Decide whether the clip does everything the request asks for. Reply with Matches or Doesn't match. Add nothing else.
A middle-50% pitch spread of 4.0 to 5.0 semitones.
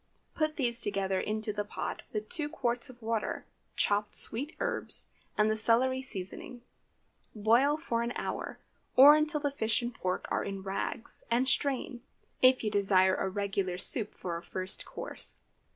Matches